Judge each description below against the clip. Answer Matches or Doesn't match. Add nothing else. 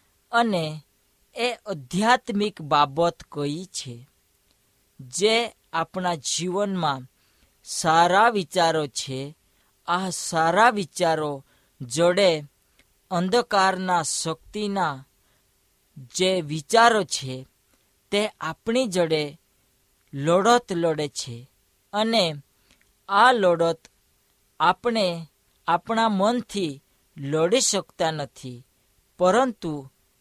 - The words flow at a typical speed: Doesn't match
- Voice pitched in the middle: Matches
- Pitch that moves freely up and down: Matches